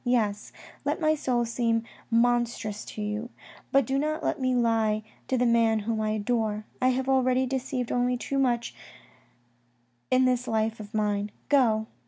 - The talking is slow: No, average, 165 wpm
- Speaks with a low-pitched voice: No, high, 240 Hz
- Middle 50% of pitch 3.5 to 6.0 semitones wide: No, average, 2.8 semitones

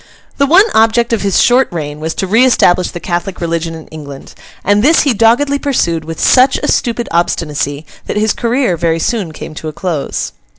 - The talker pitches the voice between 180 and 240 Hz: Yes, high, 190 Hz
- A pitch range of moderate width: No, wide, 6.6 semitones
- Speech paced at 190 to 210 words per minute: Yes, average, 200 wpm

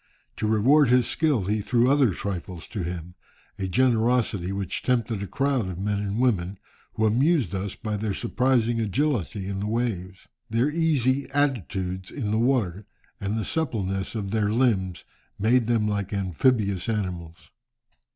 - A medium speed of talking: Yes, average, 155 wpm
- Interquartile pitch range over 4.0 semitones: Yes, average, 4.5 semitones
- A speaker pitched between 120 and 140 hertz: No, low, 110 Hz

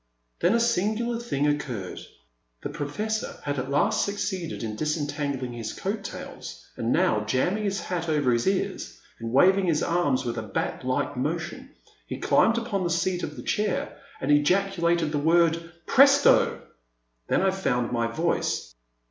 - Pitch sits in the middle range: Yes, medium, 165 Hz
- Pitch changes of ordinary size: No, wide, 6.7 semitones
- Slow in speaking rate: No, average, 165 wpm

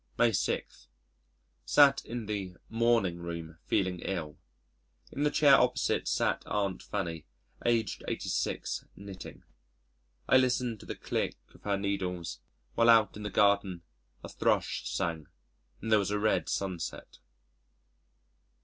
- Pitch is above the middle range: No, low, 100 Hz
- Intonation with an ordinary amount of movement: Yes, average, 4.2 semitones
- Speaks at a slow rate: Yes, slow, 130 wpm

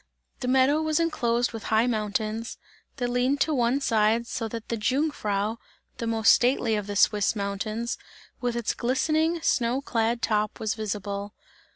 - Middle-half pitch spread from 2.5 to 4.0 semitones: Yes, average, 3.0 semitones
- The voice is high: Yes, high, 230 Hz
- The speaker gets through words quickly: No, average, 160 wpm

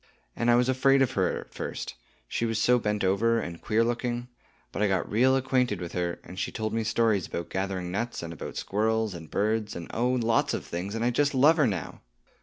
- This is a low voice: Yes, low, 110 Hz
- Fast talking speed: Yes, fast, 235 wpm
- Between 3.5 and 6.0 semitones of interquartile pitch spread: Yes, average, 4.1 semitones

